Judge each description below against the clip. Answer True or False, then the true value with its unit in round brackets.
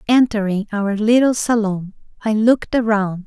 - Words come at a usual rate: False (130 wpm)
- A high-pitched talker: True (215 Hz)